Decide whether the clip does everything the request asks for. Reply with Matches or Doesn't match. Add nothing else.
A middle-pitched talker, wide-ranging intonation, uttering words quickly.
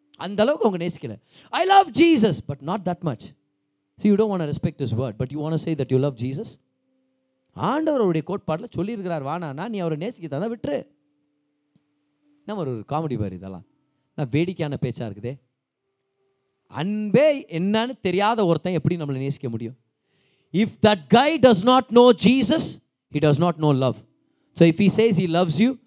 Matches